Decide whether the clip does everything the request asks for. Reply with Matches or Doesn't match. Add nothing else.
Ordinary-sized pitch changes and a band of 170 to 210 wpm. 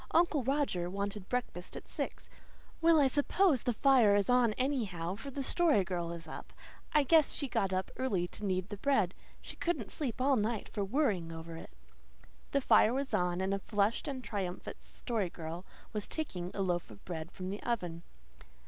Doesn't match